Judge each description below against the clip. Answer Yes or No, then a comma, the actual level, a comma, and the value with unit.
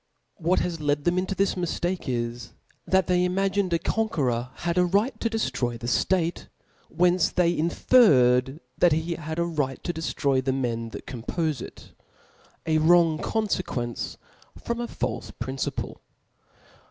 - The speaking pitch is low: No, medium, 170 Hz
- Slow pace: No, average, 155 wpm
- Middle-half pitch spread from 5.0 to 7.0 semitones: Yes, wide, 5.5 semitones